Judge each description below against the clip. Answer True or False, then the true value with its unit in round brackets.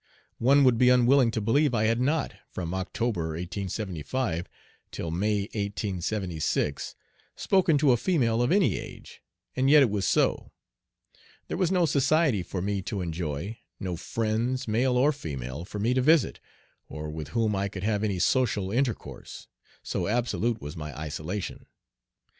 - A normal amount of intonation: False (5.9 semitones)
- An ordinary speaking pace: True (155 wpm)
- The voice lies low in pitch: True (110 Hz)